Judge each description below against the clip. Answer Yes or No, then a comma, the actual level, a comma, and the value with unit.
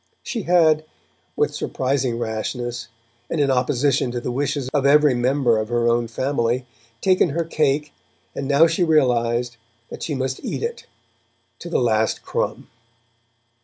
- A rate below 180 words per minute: Yes, average, 150 wpm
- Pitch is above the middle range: No, low, 130 Hz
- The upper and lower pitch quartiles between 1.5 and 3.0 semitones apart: No, average, 3.9 semitones